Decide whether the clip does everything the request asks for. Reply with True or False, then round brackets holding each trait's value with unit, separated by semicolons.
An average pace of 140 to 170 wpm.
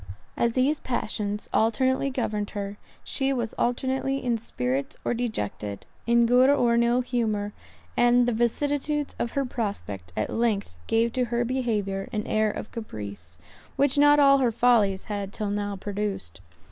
True (160 wpm)